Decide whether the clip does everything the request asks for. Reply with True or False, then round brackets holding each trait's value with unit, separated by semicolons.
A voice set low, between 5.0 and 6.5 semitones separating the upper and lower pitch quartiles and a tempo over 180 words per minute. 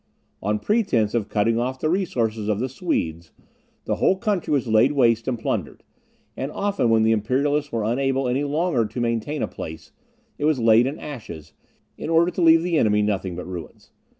True (120 Hz; 5.6 semitones; 190 wpm)